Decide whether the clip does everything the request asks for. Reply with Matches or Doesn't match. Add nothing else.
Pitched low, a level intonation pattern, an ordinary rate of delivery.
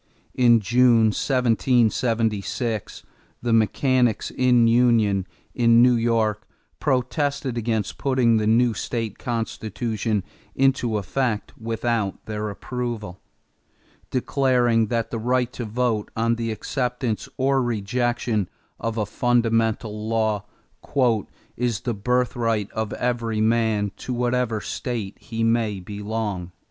Doesn't match